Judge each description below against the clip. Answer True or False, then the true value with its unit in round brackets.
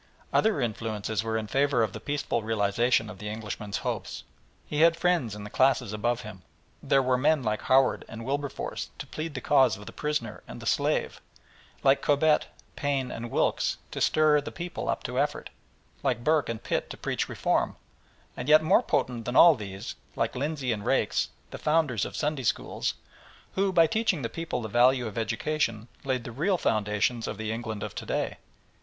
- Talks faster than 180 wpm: True (190 wpm)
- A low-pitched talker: True (125 Hz)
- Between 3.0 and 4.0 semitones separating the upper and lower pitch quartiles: False (5.1 semitones)